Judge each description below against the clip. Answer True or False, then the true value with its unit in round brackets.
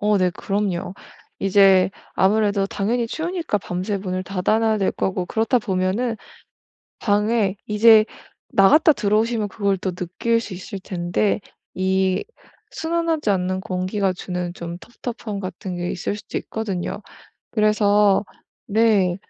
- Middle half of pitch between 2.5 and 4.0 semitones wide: True (2.8 semitones)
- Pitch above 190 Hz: True (200 Hz)